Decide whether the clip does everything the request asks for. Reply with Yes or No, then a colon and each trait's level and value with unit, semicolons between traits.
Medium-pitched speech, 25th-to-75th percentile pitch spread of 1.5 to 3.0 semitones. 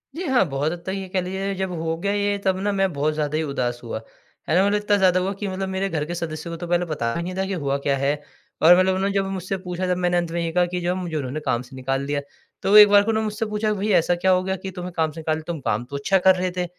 No: medium, 180 Hz; average, 3.7 semitones